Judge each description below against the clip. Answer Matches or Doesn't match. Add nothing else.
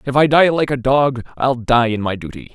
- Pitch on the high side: Doesn't match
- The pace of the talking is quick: Matches